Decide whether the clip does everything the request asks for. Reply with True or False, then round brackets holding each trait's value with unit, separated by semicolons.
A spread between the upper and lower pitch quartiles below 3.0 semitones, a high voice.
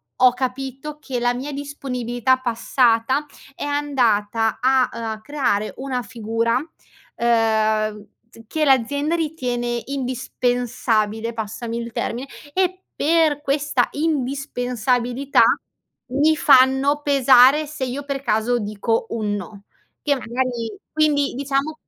False (3.6 semitones; 255 Hz)